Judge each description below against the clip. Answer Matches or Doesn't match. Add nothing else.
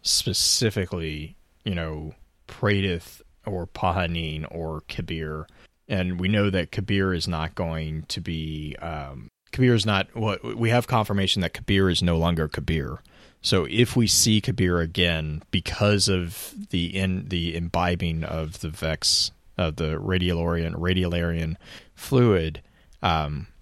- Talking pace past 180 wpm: Doesn't match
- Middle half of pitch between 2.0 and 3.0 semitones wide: Doesn't match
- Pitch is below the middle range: Matches